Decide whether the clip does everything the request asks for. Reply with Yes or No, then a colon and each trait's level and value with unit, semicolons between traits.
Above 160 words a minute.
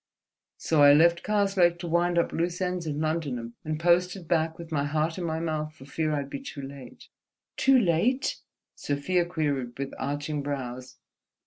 Yes: average, 175 wpm